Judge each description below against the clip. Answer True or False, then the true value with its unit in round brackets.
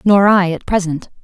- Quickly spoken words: False (195 wpm)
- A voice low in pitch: False (185 Hz)